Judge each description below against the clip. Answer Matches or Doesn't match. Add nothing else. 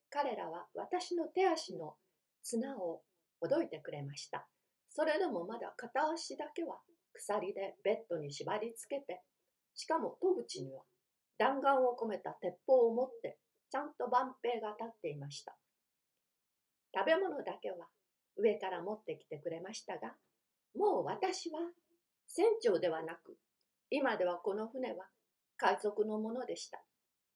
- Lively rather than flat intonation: Matches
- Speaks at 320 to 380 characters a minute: Doesn't match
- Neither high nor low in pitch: Doesn't match